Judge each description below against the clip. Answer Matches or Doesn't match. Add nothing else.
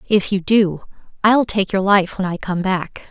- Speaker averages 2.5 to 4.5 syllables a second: Matches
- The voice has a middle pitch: Doesn't match